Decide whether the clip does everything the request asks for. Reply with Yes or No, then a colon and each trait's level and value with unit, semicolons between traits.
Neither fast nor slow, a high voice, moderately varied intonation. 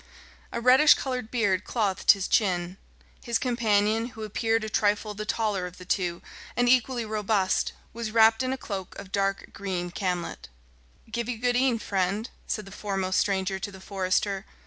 Yes: average, 170 wpm; high, 210 Hz; average, 3.2 semitones